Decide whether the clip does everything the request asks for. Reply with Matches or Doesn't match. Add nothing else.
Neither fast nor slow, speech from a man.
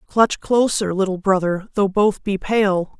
Doesn't match